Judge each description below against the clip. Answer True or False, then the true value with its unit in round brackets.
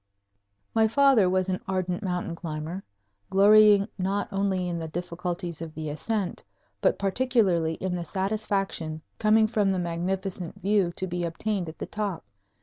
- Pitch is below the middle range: False (185 Hz)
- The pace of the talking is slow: False (150 wpm)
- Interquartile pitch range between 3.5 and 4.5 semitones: False (2.9 semitones)